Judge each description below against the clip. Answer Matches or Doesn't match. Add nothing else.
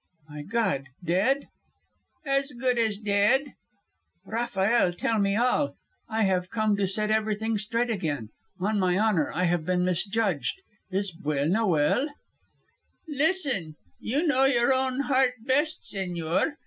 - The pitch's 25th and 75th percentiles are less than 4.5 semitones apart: Doesn't match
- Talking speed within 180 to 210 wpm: Doesn't match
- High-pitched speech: Matches